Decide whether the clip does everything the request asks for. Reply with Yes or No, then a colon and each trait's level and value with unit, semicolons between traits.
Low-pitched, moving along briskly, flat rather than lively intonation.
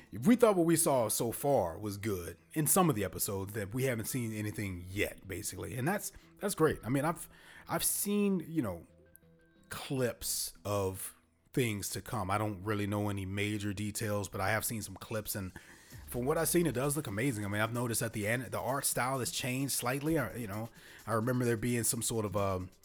No: low, 110 Hz; fast, 225 wpm; average, 5.1 semitones